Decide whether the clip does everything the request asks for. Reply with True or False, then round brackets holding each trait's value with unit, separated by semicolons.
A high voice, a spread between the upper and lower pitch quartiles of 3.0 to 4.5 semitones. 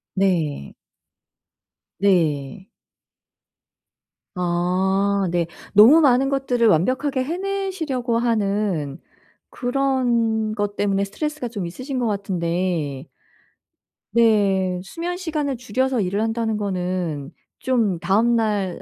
False (210 Hz; 5.5 semitones)